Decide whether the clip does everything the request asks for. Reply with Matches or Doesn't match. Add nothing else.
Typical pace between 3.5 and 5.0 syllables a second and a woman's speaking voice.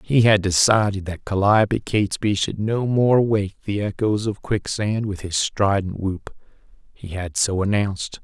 Doesn't match